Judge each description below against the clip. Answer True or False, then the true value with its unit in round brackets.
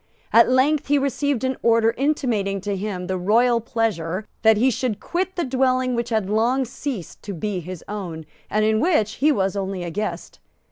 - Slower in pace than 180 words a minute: False (190 wpm)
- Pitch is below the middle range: False (225 Hz)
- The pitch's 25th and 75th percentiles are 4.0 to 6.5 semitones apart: True (4.7 semitones)